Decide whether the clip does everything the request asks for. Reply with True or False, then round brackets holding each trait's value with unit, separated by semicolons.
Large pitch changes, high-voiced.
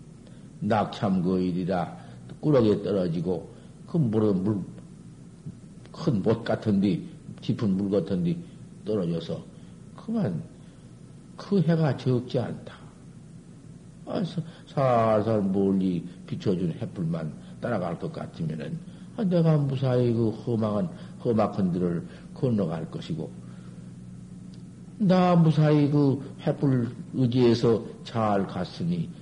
False (8.6 semitones; 130 Hz)